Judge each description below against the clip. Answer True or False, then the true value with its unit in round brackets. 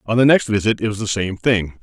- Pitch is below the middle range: True (110 Hz)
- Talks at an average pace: False (295 wpm)